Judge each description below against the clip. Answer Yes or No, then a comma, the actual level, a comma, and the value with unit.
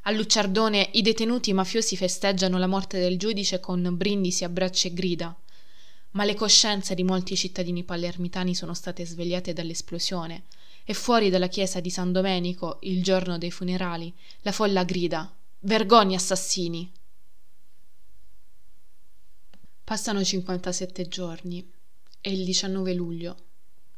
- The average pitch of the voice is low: No, medium, 185 Hz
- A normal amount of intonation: No, narrow, 1.8 semitones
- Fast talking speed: No, average, 125 wpm